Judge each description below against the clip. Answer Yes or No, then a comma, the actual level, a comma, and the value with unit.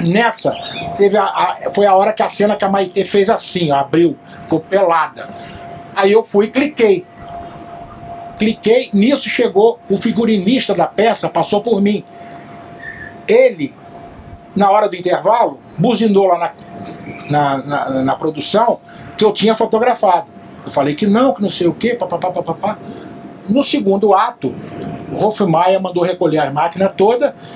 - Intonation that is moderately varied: Yes, average, 4.5 semitones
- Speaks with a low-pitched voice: No, high, 200 Hz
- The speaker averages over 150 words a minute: Yes, average, 165 wpm